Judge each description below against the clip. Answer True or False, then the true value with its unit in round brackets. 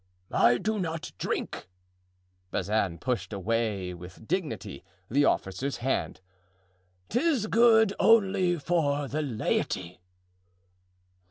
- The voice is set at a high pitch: False (115 Hz)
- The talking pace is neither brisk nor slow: False (85 wpm)